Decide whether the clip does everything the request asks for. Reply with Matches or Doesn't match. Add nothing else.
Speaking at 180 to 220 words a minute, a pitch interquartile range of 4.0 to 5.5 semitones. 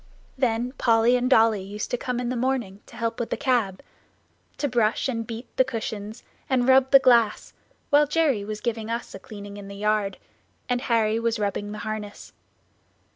Doesn't match